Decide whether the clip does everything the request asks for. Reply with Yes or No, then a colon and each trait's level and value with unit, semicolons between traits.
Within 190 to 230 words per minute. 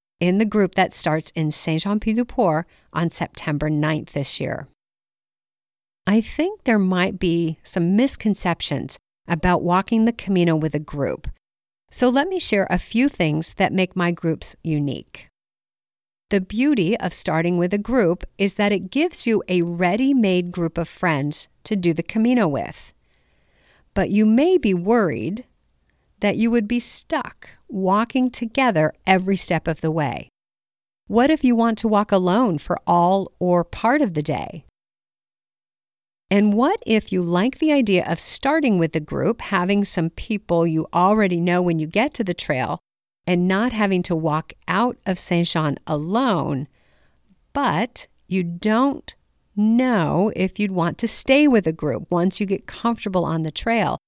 No: average, 160 wpm